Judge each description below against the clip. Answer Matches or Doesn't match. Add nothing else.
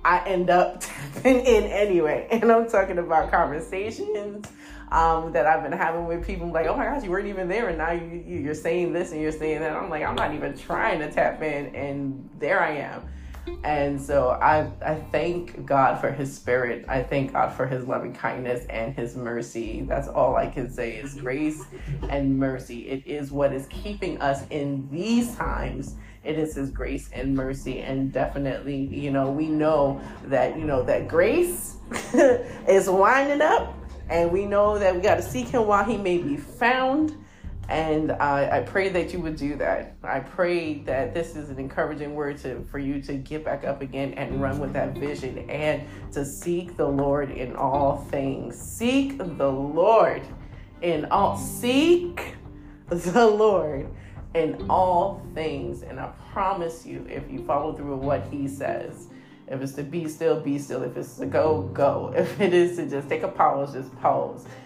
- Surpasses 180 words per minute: Matches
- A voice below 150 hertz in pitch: Doesn't match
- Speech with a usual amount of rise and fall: Matches